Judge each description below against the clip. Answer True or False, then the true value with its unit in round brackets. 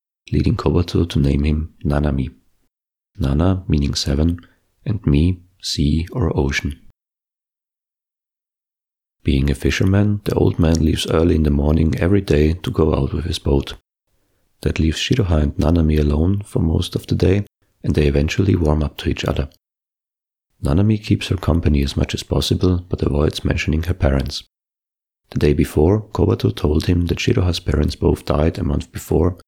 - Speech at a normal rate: True (160 wpm)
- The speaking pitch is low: True (80 Hz)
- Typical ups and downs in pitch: True (4.0 semitones)